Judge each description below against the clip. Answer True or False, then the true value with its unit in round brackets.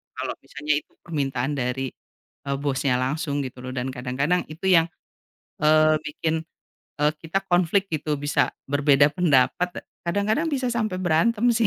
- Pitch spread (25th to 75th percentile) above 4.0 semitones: True (4.5 semitones)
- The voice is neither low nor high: True (155 Hz)